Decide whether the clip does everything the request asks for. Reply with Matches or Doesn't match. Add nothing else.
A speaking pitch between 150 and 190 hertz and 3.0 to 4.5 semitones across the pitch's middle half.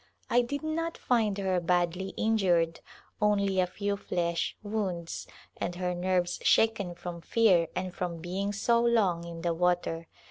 Matches